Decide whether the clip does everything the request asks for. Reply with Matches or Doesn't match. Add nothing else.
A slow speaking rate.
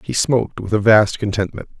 Doesn't match